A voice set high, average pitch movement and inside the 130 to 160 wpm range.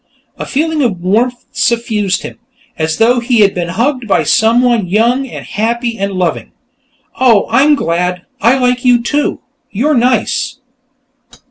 Yes: high, 235 Hz; average, 4.1 semitones; average, 145 wpm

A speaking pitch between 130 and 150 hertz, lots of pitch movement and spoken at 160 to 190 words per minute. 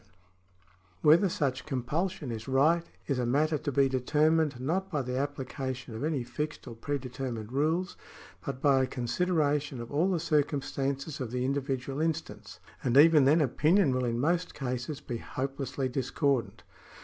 No: medium, 140 Hz; average, 3.3 semitones; average, 180 wpm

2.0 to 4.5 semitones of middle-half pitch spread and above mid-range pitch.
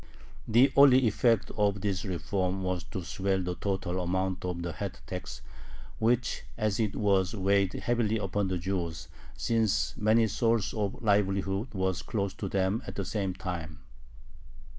No: narrow, 2.5 semitones; low, 100 Hz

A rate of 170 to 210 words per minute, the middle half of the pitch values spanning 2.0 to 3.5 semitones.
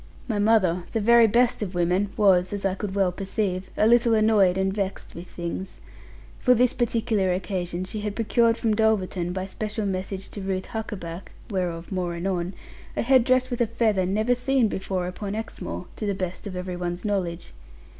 Yes: average, 185 wpm; average, 3.2 semitones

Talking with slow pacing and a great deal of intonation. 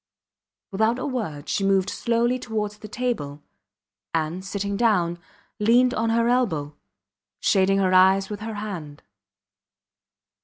No: slow, 125 wpm; average, 3.8 semitones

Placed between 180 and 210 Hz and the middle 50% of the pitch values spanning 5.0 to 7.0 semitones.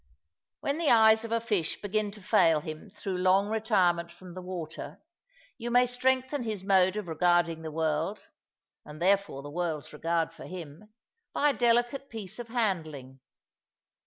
Yes: high, 190 Hz; average, 5.3 semitones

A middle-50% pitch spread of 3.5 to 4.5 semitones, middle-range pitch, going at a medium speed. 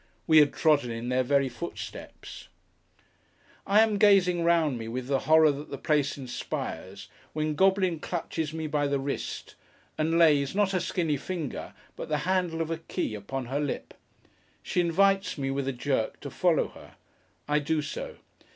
Yes: average, 3.8 semitones; medium, 150 Hz; average, 170 wpm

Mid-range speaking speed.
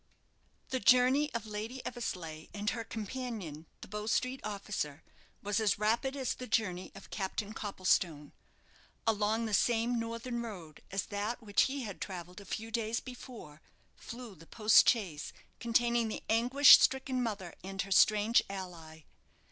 Yes: average, 150 wpm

